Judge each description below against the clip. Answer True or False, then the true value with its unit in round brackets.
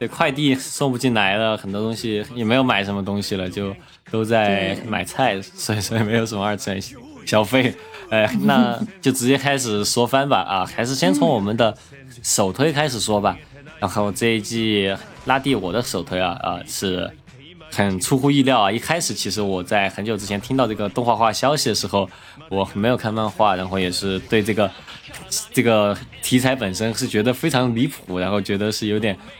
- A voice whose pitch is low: True (110 Hz)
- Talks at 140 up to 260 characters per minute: False (280 characters per minute)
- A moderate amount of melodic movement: True (3.9 semitones)